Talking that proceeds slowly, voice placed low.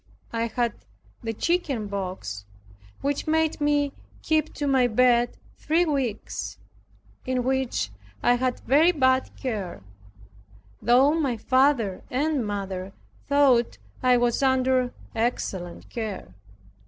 No: slow, 110 wpm; very high, 250 Hz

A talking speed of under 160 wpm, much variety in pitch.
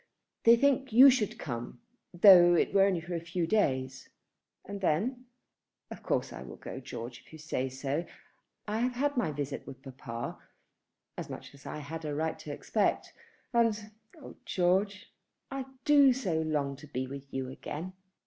No: average, 175 wpm; wide, 7.8 semitones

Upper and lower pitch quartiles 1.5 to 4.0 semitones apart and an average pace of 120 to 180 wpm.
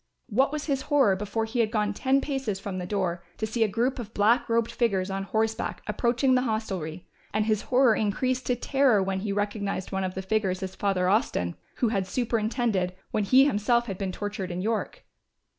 No: average, 3.7 semitones; fast, 205 wpm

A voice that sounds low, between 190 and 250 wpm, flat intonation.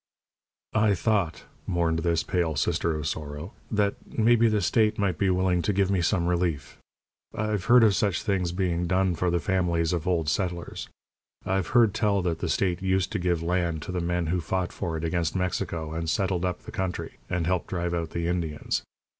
Yes: very low, 90 Hz; average, 195 wpm; narrow, 2.3 semitones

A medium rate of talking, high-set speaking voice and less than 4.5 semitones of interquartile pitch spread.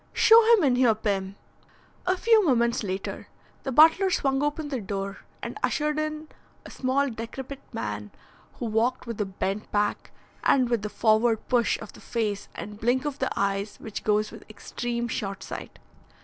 No: average, 175 wpm; high, 235 Hz; average, 4.9 semitones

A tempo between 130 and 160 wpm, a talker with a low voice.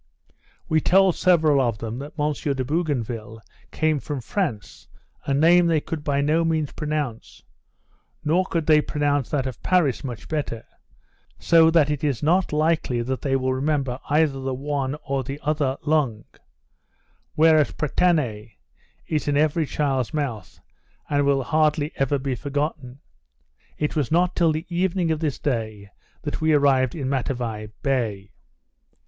No: average, 155 wpm; medium, 145 Hz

